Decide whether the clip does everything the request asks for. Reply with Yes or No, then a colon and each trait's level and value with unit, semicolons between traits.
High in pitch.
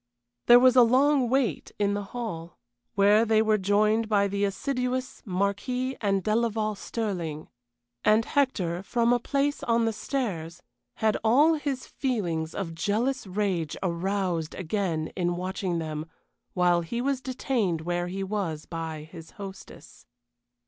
Yes: high, 205 Hz